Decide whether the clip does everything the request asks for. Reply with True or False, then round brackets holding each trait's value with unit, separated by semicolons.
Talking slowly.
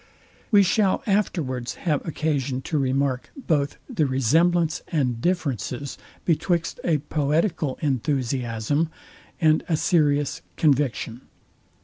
True (100 wpm)